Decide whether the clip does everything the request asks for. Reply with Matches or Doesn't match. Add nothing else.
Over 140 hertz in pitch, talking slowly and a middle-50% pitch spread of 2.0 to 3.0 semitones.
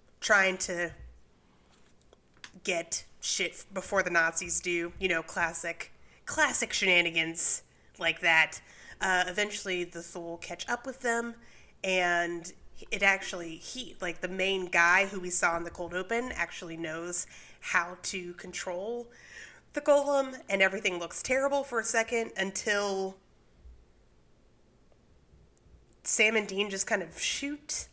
Doesn't match